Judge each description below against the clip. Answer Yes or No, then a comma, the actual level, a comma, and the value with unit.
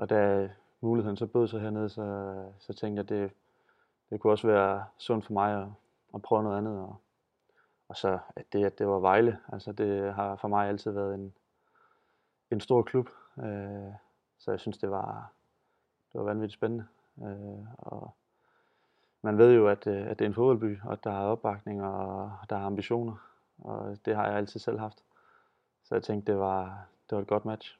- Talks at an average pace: Yes, average, 195 wpm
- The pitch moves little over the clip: Yes, narrow, 2.2 semitones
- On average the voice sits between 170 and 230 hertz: No, low, 105 Hz